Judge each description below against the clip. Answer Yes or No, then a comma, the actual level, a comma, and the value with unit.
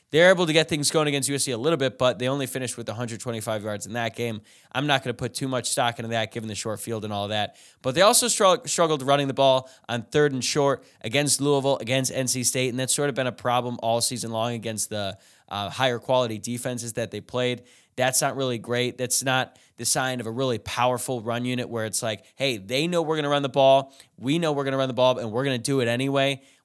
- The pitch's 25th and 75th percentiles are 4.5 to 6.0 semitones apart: No, average, 2.8 semitones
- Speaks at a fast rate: Yes, fast, 260 wpm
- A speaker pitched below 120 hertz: No, low, 125 Hz